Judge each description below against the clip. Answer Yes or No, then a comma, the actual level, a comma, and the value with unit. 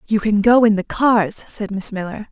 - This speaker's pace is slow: No, fast, 235 wpm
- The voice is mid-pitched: No, high, 210 Hz